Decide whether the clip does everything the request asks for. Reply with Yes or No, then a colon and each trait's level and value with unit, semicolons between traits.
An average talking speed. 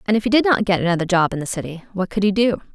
No: fast, 330 wpm